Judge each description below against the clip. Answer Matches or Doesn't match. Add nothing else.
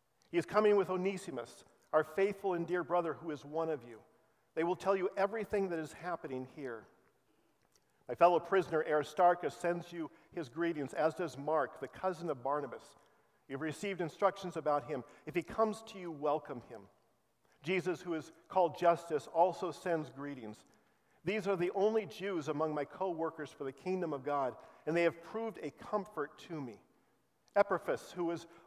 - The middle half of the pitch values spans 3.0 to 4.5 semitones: Matches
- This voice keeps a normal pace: Matches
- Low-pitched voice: Doesn't match